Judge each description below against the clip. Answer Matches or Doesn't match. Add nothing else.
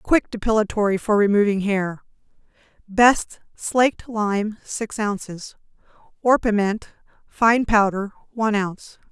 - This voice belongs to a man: Doesn't match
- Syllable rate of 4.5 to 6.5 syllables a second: Doesn't match